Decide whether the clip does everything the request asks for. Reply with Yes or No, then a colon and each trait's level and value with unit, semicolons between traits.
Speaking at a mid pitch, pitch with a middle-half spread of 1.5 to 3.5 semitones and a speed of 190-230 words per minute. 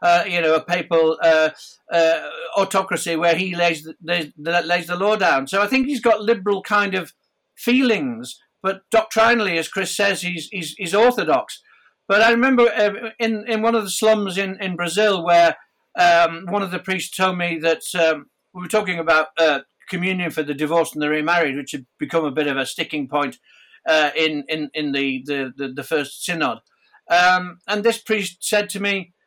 No: medium, 175 Hz; average, 4.3 semitones; average, 195 wpm